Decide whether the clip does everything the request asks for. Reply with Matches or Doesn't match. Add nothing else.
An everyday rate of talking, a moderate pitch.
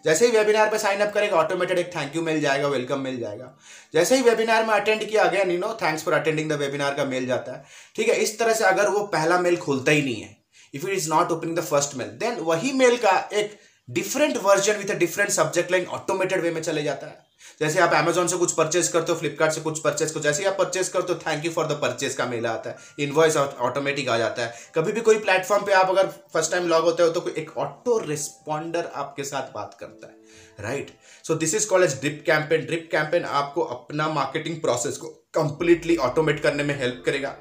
Doesn't match